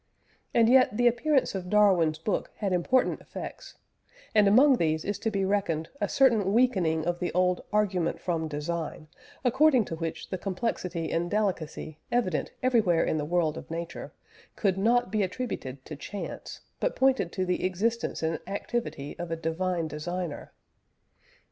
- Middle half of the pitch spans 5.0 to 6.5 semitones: Yes, average, 5.3 semitones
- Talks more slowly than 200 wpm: Yes, average, 160 wpm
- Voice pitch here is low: No, medium, 185 Hz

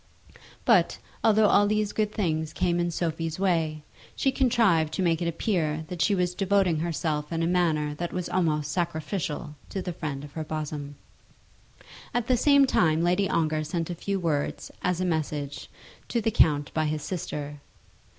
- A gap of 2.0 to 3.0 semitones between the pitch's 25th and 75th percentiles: No, average, 3.4 semitones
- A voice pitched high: No, medium, 165 Hz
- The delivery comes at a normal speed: Yes, average, 175 wpm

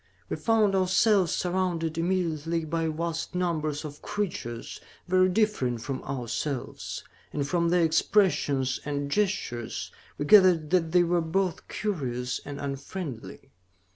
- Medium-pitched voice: Yes, medium, 165 Hz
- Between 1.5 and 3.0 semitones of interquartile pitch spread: No, average, 4.6 semitones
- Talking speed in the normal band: No, slow, 125 wpm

